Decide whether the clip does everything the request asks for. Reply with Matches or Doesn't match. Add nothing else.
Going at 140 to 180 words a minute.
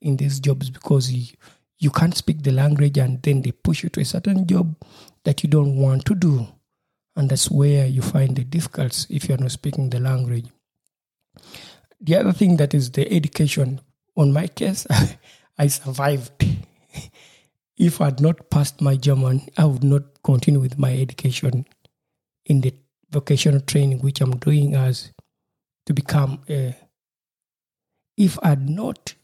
Matches